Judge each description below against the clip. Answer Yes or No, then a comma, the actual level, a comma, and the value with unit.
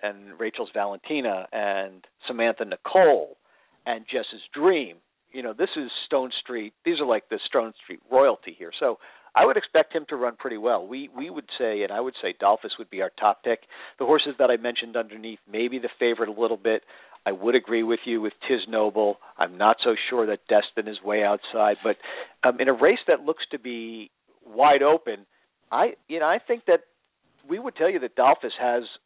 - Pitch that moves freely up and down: Yes, wide, 6.4 semitones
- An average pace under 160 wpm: No, fast, 205 wpm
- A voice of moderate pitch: No, low, 115 Hz